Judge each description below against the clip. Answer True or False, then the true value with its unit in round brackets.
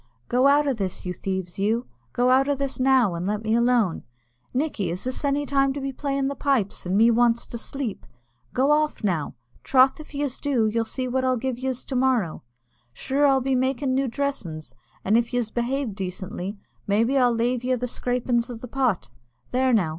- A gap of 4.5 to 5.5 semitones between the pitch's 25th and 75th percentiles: False (3.7 semitones)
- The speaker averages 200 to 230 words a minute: True (205 wpm)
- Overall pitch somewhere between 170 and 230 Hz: False (250 Hz)